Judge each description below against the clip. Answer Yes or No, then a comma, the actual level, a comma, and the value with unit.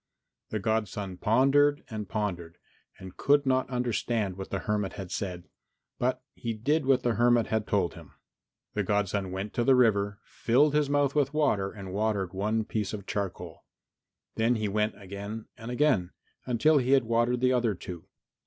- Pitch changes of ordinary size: Yes, average, 4.1 semitones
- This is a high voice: No, low, 110 Hz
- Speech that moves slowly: No, average, 175 wpm